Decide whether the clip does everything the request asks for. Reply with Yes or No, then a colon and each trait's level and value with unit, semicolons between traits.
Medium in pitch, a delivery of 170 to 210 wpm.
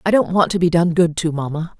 No: medium, 170 Hz; fast, 300 wpm